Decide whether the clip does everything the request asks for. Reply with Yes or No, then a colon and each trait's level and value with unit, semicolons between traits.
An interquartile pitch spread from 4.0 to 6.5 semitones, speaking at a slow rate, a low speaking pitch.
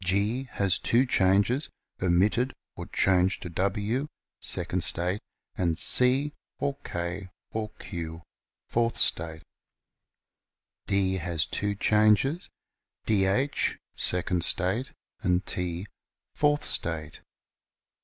Yes: average, 4.8 semitones; slow, 105 wpm; very low, 95 Hz